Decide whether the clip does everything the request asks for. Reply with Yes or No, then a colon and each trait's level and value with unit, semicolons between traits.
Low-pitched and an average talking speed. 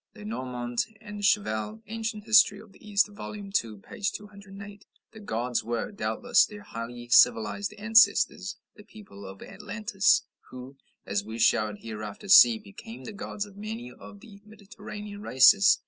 No: high, 200 Hz; average, 145 wpm